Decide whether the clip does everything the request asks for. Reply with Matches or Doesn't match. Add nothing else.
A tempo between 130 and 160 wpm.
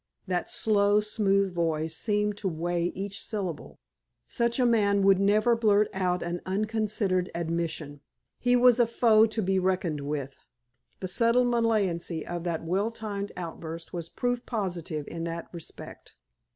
Matches